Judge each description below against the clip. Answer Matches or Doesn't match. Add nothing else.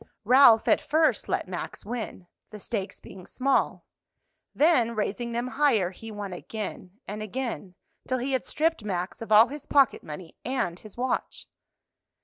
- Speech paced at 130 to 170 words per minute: Matches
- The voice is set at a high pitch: Matches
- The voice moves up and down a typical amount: Matches